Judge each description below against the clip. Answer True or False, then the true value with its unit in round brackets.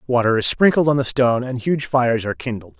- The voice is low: True (125 Hz)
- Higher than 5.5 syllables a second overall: True (6.4 syllables/s)